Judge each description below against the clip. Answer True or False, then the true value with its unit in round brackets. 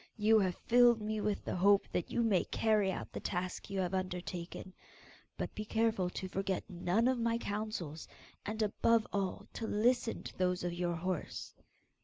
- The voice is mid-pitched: False (200 Hz)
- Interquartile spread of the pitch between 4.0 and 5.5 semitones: False (3.4 semitones)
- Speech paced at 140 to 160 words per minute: False (180 wpm)